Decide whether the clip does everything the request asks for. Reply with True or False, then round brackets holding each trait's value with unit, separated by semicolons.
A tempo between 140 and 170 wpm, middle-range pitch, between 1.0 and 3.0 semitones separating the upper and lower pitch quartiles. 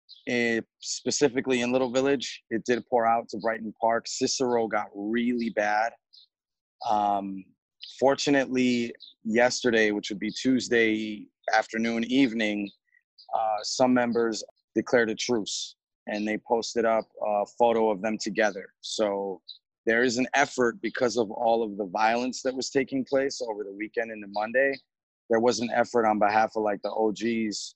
False (155 wpm; 115 Hz; 2.7 semitones)